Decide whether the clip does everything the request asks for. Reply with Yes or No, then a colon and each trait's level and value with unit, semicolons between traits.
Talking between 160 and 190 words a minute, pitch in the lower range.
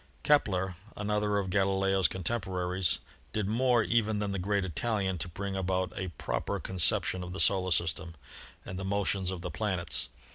Yes: average, 170 wpm; very low, 95 Hz